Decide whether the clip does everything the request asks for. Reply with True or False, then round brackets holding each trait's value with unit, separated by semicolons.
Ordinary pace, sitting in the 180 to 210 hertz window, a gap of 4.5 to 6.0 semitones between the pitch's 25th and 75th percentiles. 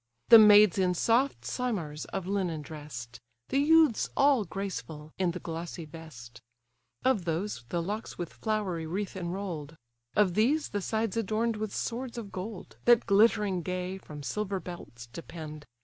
True (150 wpm; 190 Hz; 4.9 semitones)